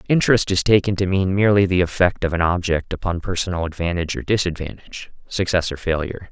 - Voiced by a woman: No, male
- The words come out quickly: No, average, 180 wpm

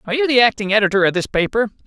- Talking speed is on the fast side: Yes, fast, 255 wpm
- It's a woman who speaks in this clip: No, male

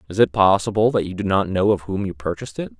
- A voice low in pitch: Yes, very low, 95 Hz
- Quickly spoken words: Yes, fast, 280 wpm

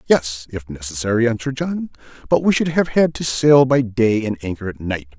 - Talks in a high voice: No, low, 120 Hz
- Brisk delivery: Yes, fast, 210 wpm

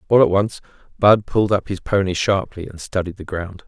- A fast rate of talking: Yes, fast, 210 wpm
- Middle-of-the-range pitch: No, very low, 95 Hz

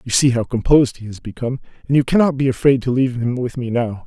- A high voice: No, low, 125 Hz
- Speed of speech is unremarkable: No, fast, 265 wpm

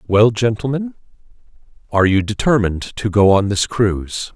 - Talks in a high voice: No, low, 110 Hz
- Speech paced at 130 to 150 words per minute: Yes, average, 140 wpm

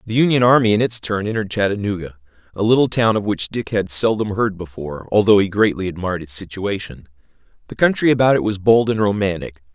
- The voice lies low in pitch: Yes, low, 100 Hz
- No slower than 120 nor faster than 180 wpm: No, average, 195 wpm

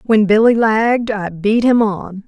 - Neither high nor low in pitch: No, high, 215 Hz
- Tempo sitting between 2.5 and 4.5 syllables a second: Yes, 4.2 syllables/s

